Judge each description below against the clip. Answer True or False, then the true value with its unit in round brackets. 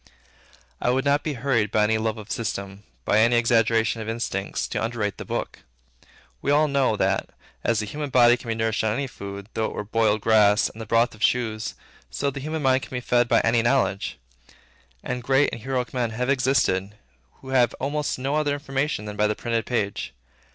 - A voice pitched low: True (115 Hz)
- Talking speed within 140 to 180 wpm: False (205 wpm)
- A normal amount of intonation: True (3.6 semitones)